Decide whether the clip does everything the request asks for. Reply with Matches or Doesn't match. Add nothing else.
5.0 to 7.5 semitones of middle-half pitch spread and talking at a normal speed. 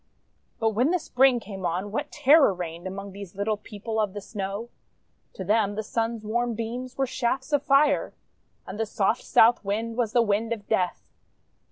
Doesn't match